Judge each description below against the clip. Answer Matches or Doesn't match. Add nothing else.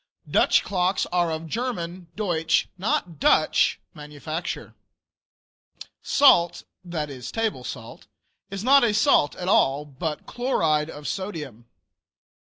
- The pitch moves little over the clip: Doesn't match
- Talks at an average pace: Doesn't match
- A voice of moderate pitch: Matches